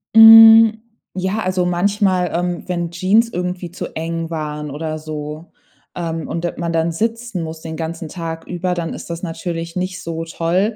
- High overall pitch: No, medium, 175 Hz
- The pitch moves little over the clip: Yes, narrow, 2.2 semitones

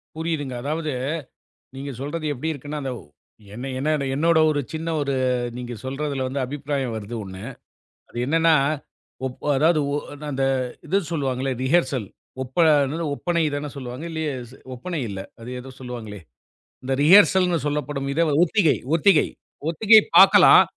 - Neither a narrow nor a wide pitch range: Yes, average, 3.6 semitones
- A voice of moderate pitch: Yes, medium, 145 Hz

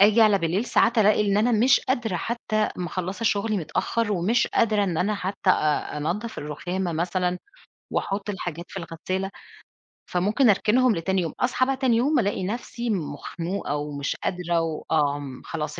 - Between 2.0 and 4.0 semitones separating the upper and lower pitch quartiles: No, average, 4.7 semitones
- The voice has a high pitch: Yes, high, 195 Hz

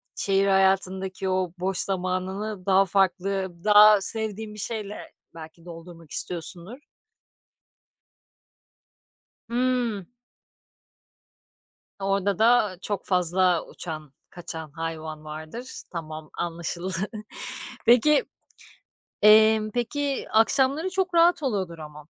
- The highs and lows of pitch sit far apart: No, average, 4.1 semitones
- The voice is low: No, high, 190 Hz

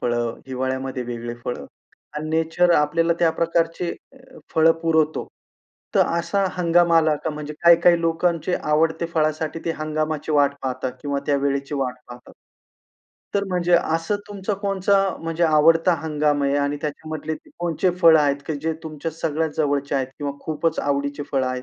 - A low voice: No, medium, 155 Hz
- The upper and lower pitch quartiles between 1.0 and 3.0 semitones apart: Yes, average, 2.7 semitones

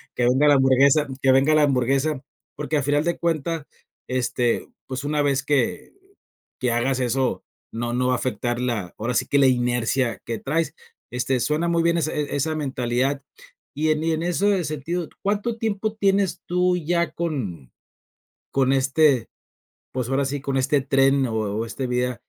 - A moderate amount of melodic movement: Yes, average, 3.9 semitones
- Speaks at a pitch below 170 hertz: Yes, low, 135 Hz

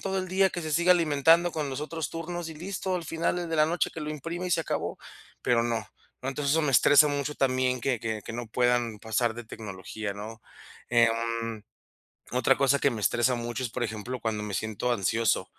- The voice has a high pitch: No, low, 130 Hz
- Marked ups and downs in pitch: Yes, wide, 5.9 semitones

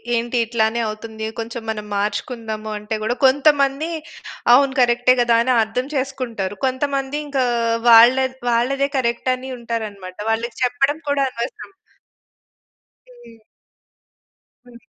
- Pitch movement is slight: No, average, 3.1 semitones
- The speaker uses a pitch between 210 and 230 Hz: No, high, 240 Hz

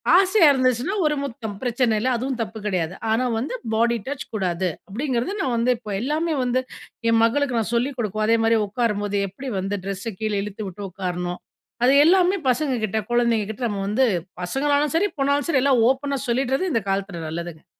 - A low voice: No, high, 235 Hz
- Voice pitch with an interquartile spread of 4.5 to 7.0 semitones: Yes, average, 4.9 semitones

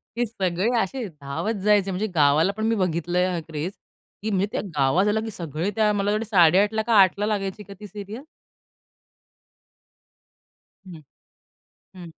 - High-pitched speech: Yes, high, 195 Hz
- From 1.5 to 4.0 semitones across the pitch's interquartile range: Yes, average, 3.5 semitones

